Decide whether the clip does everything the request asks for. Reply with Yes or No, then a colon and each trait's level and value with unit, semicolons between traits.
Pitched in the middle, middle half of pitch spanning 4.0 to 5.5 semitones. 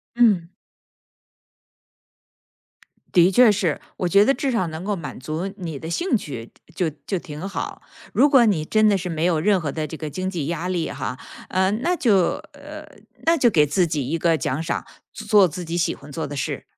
Yes: medium, 175 Hz; average, 4.9 semitones